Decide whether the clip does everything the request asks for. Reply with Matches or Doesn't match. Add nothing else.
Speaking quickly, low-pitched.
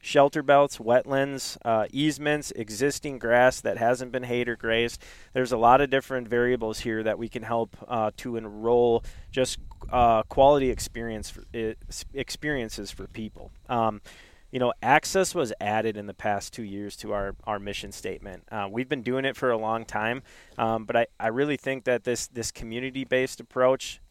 Doesn't match